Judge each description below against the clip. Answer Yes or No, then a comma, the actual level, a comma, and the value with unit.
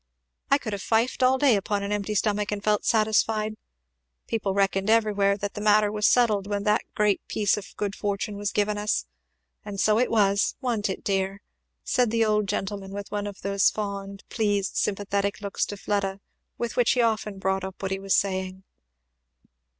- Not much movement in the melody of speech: Yes, narrow, 1.4 semitones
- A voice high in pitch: Yes, high, 205 Hz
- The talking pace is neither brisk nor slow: Yes, average, 190 wpm